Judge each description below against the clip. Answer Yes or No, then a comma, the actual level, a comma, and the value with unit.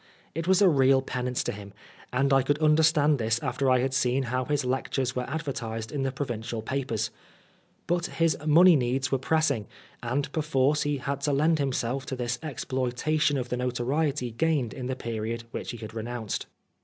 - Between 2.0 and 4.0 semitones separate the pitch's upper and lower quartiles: Yes, average, 3.4 semitones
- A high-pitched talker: No, low, 135 Hz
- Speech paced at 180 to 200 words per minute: Yes, average, 185 wpm